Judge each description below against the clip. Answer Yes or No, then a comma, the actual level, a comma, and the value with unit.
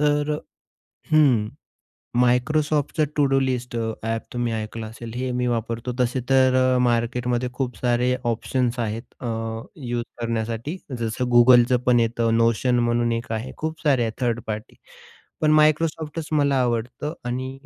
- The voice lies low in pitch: Yes, low, 125 Hz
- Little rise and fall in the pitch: Yes, narrow, 2.3 semitones